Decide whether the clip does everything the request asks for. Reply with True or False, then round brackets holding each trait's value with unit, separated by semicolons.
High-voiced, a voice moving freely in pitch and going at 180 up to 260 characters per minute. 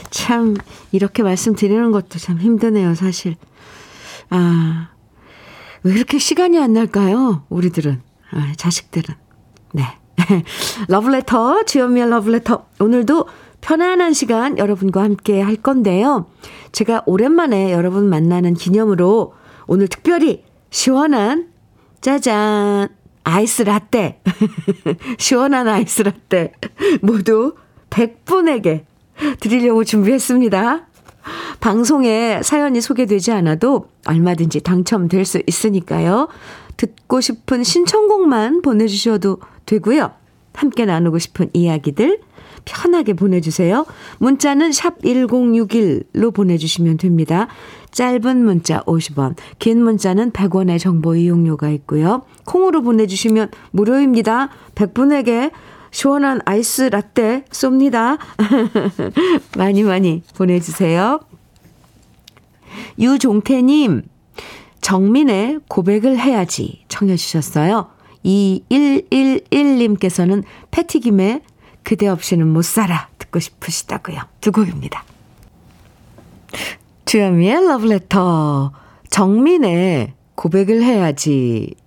True (210 Hz; 6.1 semitones; 240 characters per minute)